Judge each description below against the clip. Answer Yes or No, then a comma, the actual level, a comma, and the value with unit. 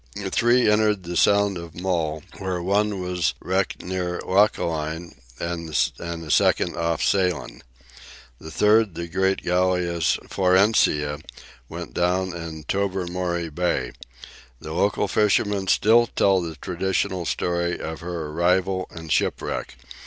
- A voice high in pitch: No, very low, 90 Hz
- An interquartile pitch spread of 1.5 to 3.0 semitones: Yes, narrow, 2.4 semitones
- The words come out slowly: Yes, slow, 125 wpm